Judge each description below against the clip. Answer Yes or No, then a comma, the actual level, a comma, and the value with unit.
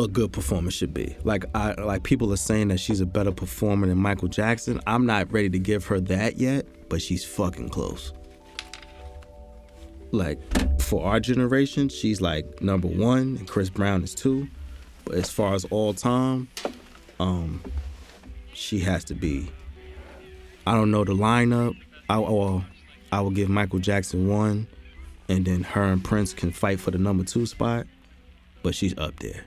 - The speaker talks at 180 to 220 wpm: No, average, 170 wpm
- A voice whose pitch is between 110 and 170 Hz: No, very low, 95 Hz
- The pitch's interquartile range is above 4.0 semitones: Yes, average, 4.4 semitones